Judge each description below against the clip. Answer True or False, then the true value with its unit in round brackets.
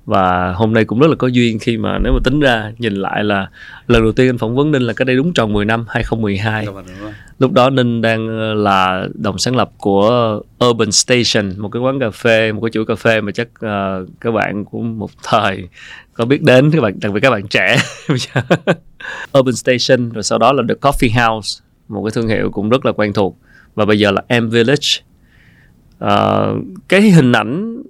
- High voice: False (115 Hz)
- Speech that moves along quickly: False (215 wpm)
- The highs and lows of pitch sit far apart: False (3.4 semitones)